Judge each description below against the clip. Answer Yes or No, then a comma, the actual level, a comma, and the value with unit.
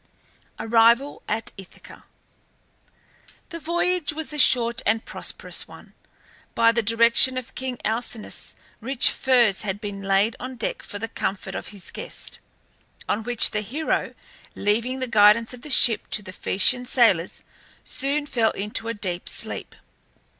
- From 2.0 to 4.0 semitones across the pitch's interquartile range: Yes, average, 3.6 semitones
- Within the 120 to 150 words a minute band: Yes, average, 145 wpm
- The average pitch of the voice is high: Yes, high, 230 Hz